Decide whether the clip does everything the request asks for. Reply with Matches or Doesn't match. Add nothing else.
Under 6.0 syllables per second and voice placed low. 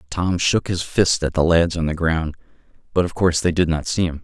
Matches